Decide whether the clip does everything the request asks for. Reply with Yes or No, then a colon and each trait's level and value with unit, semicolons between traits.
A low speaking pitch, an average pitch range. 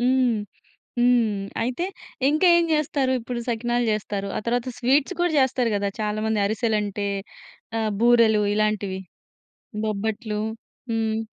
No: high, 230 Hz; average, 3.0 semitones